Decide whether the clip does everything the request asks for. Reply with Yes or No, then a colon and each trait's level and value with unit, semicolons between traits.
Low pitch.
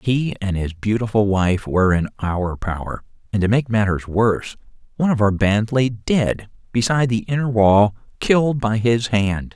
Yes: low, 110 Hz